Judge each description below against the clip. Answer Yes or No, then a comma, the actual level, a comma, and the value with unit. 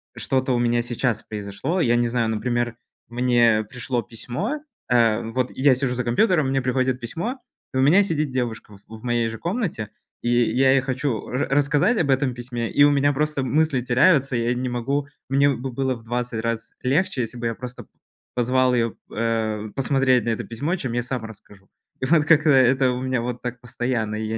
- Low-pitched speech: Yes, low, 125 Hz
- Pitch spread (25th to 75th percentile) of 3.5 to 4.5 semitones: No, narrow, 2.6 semitones